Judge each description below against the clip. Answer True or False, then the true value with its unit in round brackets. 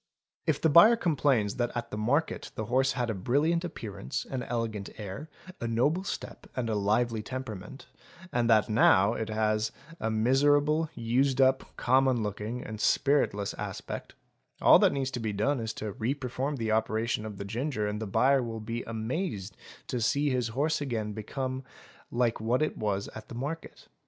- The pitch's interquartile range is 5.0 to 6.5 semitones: False (3.7 semitones)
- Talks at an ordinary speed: True (175 wpm)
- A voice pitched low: True (120 Hz)